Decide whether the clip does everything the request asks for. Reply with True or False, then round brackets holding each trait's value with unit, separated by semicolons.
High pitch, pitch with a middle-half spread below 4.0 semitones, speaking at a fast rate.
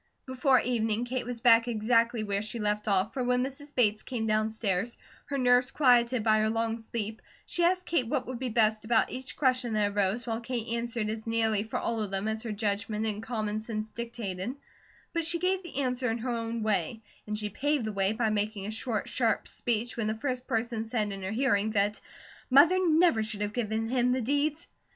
True (230 Hz; 2.6 semitones; 210 wpm)